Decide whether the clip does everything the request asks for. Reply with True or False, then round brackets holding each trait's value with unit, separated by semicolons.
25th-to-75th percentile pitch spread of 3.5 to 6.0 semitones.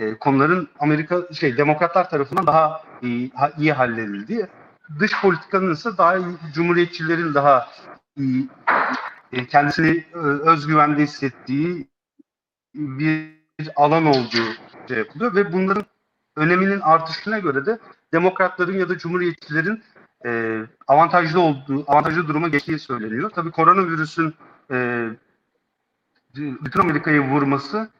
True (3.9 semitones)